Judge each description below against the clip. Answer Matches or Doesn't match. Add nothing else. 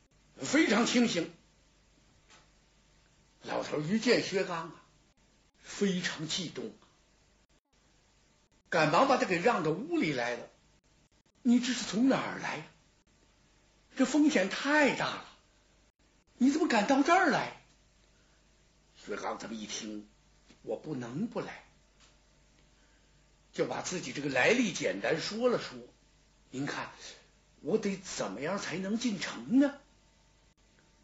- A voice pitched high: Matches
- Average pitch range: Doesn't match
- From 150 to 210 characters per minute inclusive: Matches